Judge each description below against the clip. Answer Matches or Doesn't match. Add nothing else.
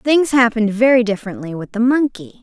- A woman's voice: Matches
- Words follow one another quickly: Doesn't match